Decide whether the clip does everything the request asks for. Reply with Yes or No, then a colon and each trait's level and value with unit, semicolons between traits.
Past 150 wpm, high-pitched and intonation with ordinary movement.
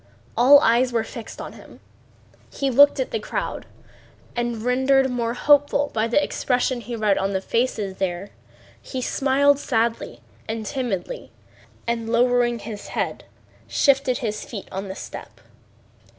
No: average, 145 wpm; high, 240 Hz; average, 3.1 semitones